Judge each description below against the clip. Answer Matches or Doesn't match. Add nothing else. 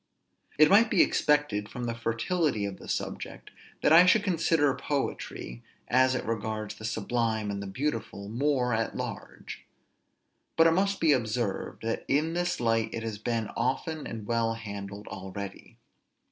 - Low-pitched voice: Matches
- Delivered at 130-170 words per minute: Matches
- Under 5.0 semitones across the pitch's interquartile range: Doesn't match